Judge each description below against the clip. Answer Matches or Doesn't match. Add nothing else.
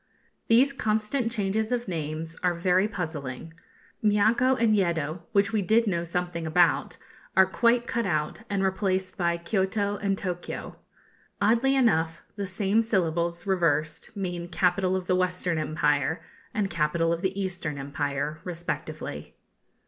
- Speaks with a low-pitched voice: Doesn't match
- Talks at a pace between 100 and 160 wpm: Matches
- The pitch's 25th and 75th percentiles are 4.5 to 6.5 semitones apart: Doesn't match